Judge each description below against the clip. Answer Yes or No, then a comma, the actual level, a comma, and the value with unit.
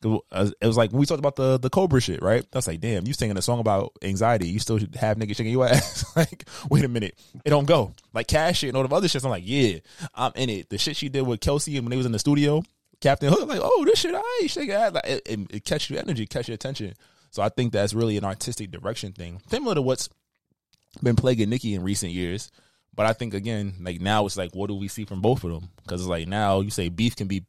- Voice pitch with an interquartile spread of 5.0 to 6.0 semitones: Yes, wide, 5.5 semitones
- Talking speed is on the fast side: Yes, fast, 265 wpm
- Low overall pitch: Yes, low, 115 Hz